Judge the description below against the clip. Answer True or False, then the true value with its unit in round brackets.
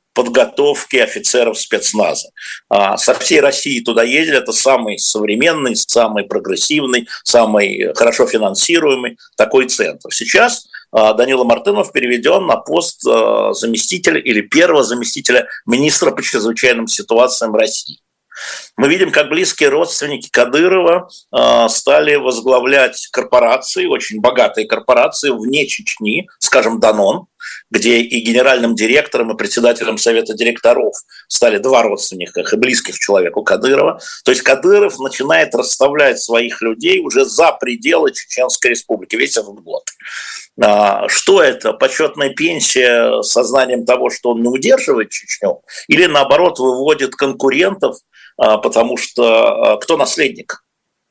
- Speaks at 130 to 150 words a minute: False (115 wpm)